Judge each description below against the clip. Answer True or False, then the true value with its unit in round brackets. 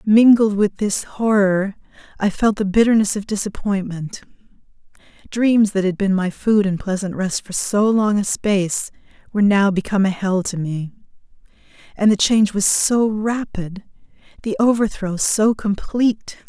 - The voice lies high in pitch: True (205 Hz)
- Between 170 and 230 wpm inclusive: False (150 wpm)